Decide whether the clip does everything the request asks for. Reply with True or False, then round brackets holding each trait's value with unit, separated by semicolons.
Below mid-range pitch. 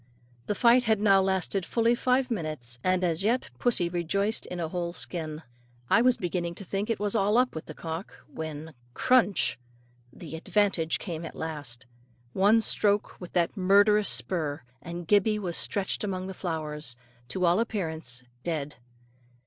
False (185 Hz)